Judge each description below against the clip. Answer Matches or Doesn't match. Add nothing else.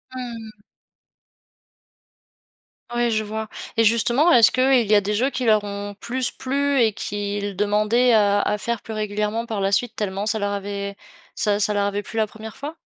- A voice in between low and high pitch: Doesn't match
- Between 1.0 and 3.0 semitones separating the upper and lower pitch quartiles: Matches